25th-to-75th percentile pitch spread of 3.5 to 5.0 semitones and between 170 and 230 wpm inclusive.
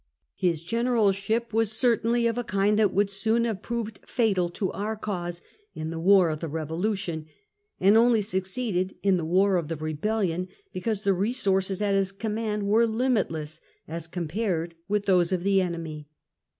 Yes: average, 4.1 semitones; average, 175 wpm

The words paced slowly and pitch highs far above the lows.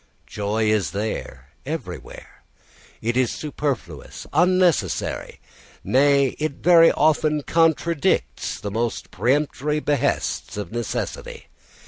Yes: slow, 95 wpm; wide, 5.8 semitones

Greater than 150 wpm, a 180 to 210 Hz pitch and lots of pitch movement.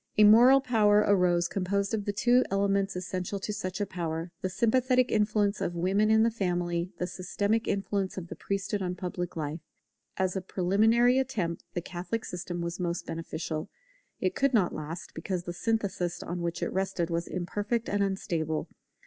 No: average, 180 wpm; high, 190 Hz; average, 3.2 semitones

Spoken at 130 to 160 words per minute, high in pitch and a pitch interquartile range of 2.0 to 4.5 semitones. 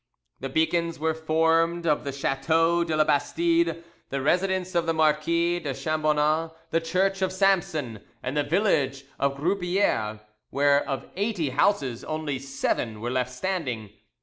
No: average, 150 wpm; medium, 160 Hz; average, 3.8 semitones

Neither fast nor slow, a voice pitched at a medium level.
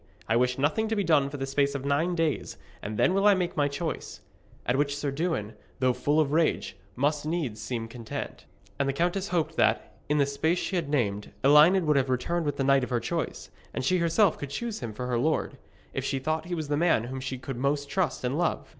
No: fast, 240 wpm; medium, 145 Hz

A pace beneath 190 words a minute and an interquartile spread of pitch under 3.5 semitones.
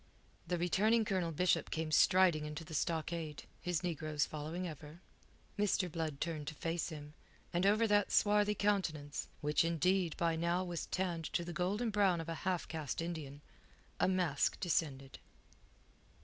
Yes: average, 155 wpm; average, 3.1 semitones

